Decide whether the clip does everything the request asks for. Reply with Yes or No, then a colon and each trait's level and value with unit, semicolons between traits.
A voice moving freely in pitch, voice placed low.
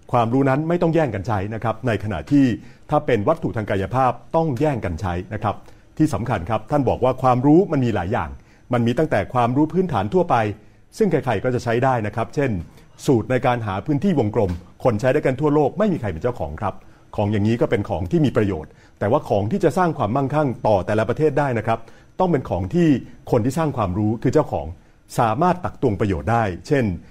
Yes: wide, 5.9 semitones; low, 120 Hz